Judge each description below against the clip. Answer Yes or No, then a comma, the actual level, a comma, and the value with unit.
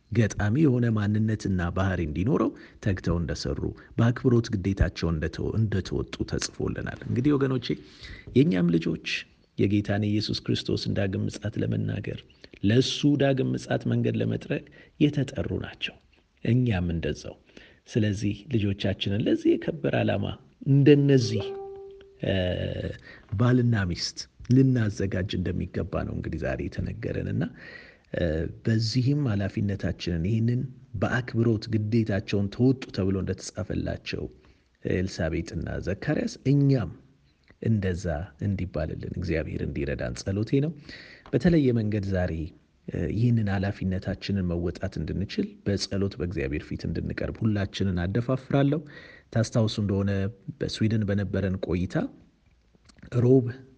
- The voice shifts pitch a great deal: No, average, 4.8 semitones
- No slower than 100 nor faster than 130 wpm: No, average, 90 wpm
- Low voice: Yes, low, 100 Hz